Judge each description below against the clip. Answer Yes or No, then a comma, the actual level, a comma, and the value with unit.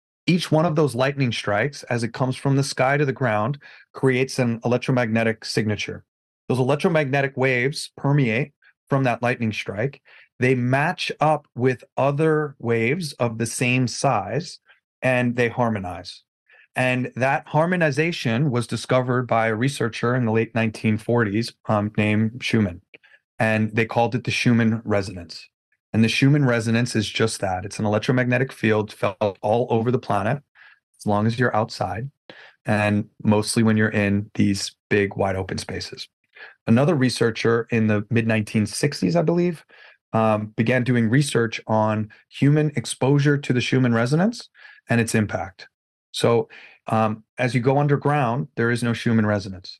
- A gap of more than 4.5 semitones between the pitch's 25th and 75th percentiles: No, average, 3.7 semitones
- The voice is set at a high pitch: No, low, 120 Hz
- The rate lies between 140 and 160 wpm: Yes, average, 150 wpm